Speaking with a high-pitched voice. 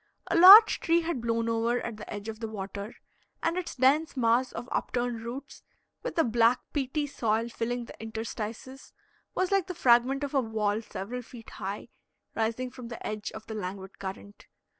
Yes: high, 235 Hz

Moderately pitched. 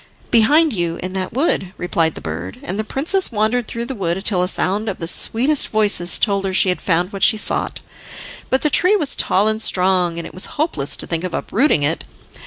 No: high, 195 Hz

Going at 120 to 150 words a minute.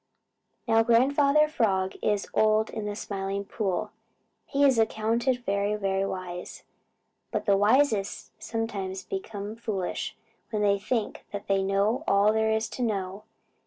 Yes: average, 145 wpm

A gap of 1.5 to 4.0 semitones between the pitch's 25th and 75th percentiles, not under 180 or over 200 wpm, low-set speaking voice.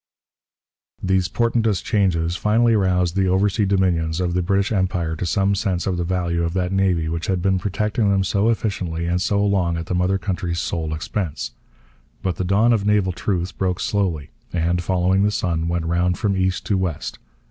Yes: narrow, 2.5 semitones; average, 190 wpm; very low, 95 Hz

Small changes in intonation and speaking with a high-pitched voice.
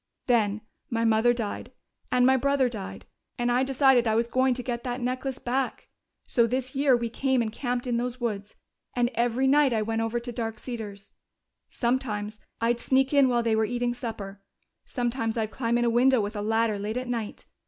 Yes: narrow, 2.2 semitones; high, 240 Hz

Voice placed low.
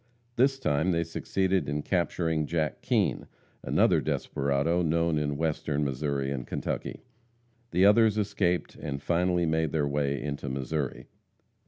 Yes: very low, 80 Hz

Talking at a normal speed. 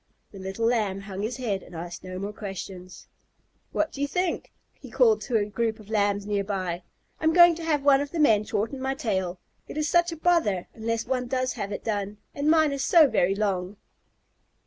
No: fast, 215 wpm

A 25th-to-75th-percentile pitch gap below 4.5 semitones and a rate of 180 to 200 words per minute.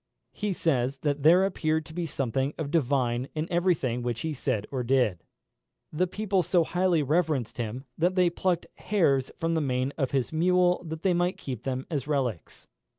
No: average, 5.2 semitones; average, 190 wpm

